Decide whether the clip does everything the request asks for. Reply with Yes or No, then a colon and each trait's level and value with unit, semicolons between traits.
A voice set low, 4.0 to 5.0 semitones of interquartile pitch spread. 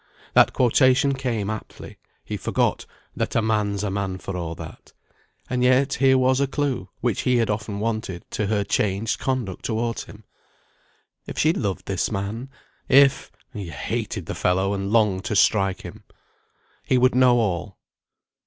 Yes: low, 110 Hz; average, 4.4 semitones